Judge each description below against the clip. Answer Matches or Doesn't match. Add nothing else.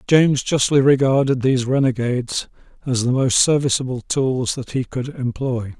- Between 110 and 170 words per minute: Matches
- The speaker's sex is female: Doesn't match